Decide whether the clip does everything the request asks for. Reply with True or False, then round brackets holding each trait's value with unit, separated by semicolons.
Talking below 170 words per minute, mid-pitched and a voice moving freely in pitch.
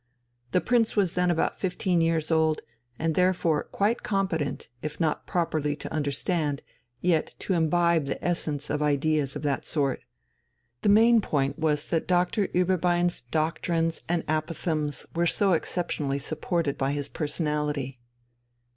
False (140 wpm; 160 Hz; 3.0 semitones)